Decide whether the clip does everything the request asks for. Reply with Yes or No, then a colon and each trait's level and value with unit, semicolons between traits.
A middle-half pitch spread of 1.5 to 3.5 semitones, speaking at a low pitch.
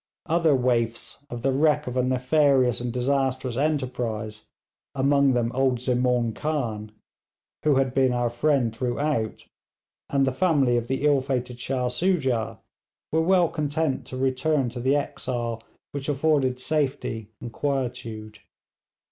Yes: average, 2.8 semitones; low, 130 Hz